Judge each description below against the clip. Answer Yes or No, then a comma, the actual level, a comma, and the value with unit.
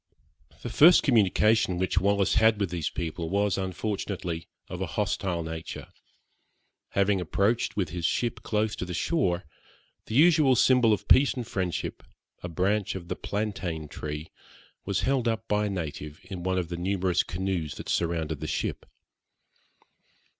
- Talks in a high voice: No, very low, 95 Hz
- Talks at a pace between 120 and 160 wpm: Yes, average, 155 wpm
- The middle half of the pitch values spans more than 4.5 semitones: No, average, 3.7 semitones